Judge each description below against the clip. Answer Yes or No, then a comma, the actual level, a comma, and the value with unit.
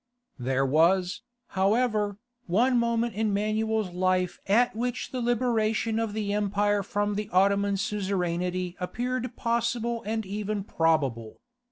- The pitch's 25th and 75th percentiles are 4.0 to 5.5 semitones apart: No, average, 3.5 semitones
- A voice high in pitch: Yes, high, 205 Hz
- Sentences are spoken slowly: Yes, slow, 125 wpm